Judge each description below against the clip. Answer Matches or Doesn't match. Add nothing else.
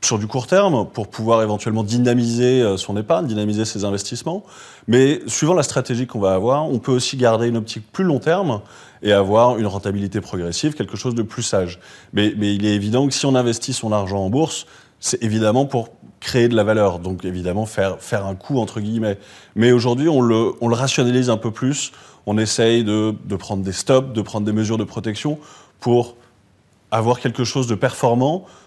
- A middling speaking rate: Matches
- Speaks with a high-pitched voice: Doesn't match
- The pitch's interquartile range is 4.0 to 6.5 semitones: Doesn't match